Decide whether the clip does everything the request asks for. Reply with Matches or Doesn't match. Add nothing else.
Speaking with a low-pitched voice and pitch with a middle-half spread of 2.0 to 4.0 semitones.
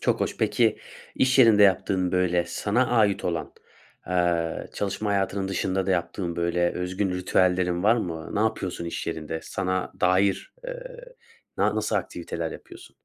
Matches